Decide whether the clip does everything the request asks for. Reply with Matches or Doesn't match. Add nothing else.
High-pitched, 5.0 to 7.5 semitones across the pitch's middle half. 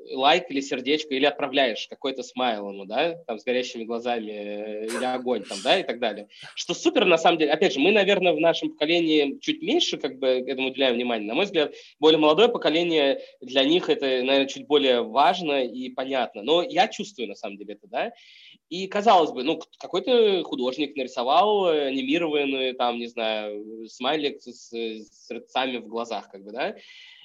Doesn't match